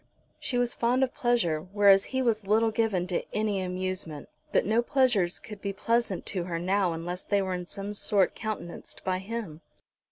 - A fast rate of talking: No, average, 185 wpm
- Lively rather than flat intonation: No, average, 3.9 semitones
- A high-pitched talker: Yes, high, 200 Hz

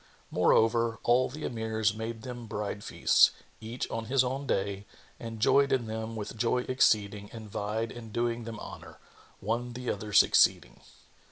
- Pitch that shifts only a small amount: Yes, narrow, 2.0 semitones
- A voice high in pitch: No, low, 115 Hz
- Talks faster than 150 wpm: Yes, average, 160 wpm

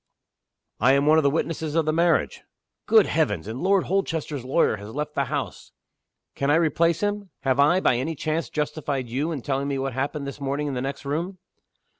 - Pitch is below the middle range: No, medium, 145 Hz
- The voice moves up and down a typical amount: Yes, average, 3.2 semitones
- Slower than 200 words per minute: No, fast, 205 wpm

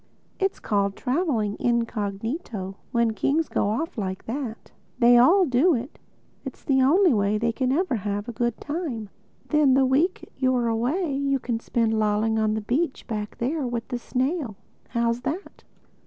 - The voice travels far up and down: No, average, 4.2 semitones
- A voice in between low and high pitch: No, high, 240 Hz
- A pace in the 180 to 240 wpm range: No, average, 160 wpm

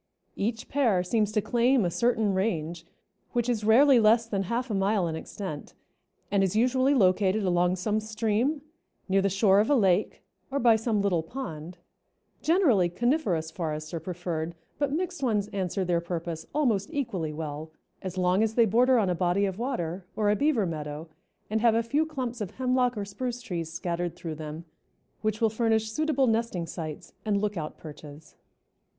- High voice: Yes, high, 205 Hz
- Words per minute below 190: Yes, average, 180 wpm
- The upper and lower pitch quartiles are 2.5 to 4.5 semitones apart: No, average, 5.2 semitones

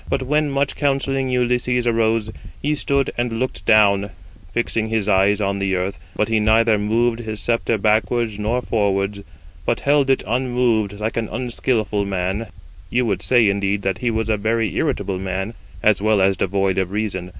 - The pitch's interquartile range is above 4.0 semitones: No, average, 3.2 semitones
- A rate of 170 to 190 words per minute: Yes, average, 175 wpm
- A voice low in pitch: Yes, low, 110 Hz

